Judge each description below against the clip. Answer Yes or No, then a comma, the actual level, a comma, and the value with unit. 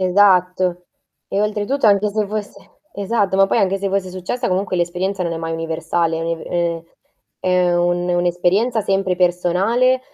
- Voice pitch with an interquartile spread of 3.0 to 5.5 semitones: No, narrow, 2.4 semitones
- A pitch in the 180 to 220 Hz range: Yes, medium, 185 Hz